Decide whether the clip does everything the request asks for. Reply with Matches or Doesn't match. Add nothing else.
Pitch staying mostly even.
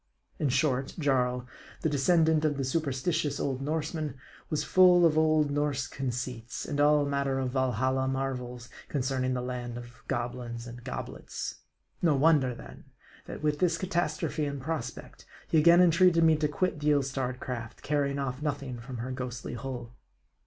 Doesn't match